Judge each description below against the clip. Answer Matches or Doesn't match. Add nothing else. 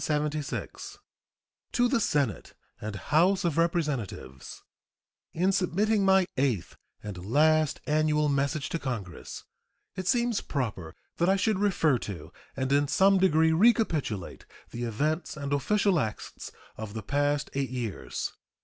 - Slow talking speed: Matches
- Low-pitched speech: Doesn't match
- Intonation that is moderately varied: Doesn't match